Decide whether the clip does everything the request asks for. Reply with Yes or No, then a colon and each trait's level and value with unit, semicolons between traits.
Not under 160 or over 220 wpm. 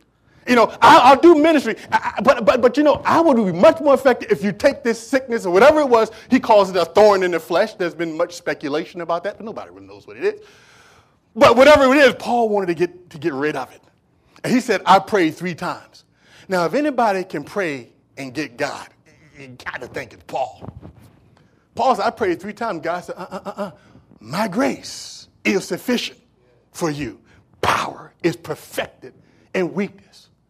Yes: average, 200 wpm